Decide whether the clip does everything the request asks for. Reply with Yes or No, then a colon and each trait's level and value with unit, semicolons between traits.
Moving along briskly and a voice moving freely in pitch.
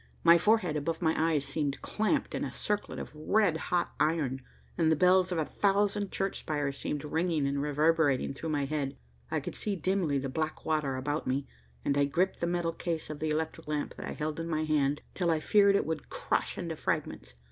No: fast, 210 wpm; average, 3.2 semitones